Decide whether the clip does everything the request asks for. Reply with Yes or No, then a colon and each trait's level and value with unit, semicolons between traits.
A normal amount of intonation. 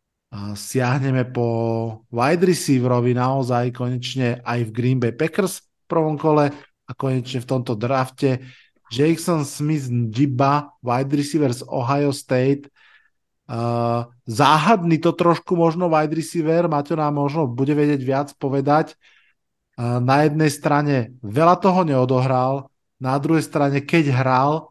Yes: average, 3.6 semitones